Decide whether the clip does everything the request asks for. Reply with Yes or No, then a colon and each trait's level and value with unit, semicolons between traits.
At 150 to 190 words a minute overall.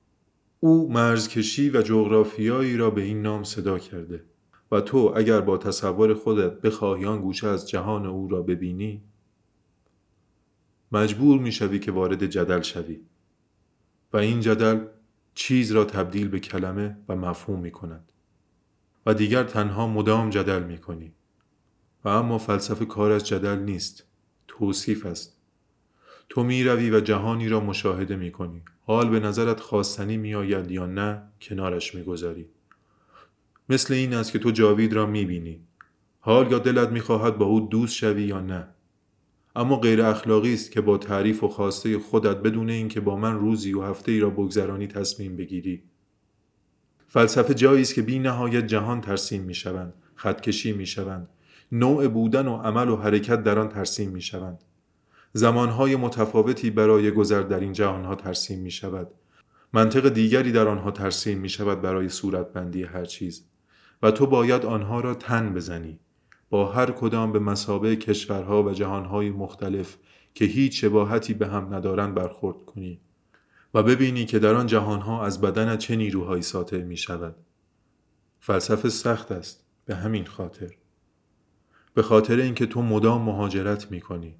Yes: fast, 155 wpm